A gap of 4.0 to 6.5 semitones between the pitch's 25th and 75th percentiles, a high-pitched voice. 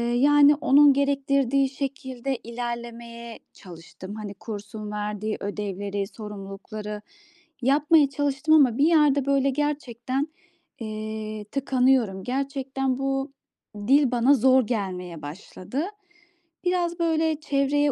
Yes: average, 4.7 semitones; very high, 255 Hz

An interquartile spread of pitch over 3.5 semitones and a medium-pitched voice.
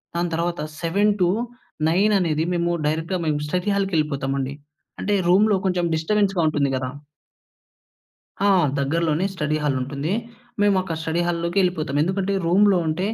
Yes: average, 3.9 semitones; medium, 170 Hz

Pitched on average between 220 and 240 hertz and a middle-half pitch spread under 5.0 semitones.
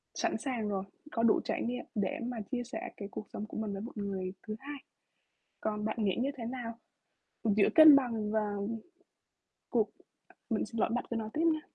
Yes: high, 225 Hz; average, 2.8 semitones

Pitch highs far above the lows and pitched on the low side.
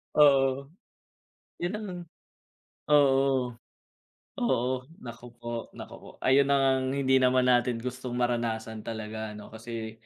No: narrow, 2.6 semitones; low, 125 Hz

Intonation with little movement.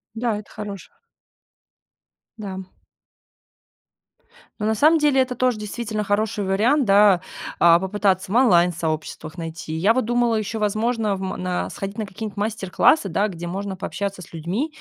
No: average, 3.2 semitones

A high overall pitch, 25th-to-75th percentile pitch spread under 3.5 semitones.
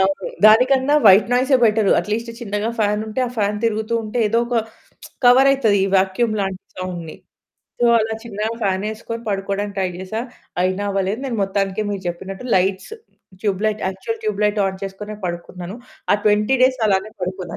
Yes: high, 210 Hz; average, 2.9 semitones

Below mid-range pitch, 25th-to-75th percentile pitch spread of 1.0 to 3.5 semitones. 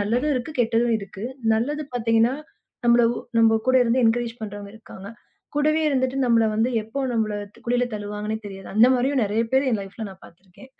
No: high, 230 Hz; average, 3.1 semitones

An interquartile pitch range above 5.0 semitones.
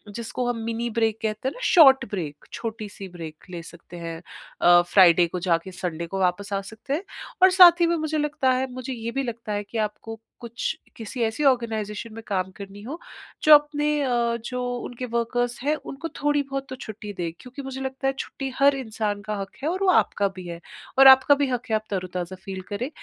Yes: wide, 5.4 semitones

